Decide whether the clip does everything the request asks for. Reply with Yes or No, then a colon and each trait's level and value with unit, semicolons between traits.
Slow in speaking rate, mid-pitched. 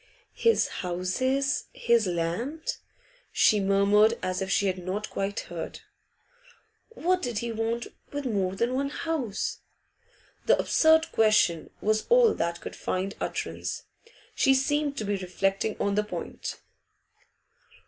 No: slow, 130 wpm; high, 215 Hz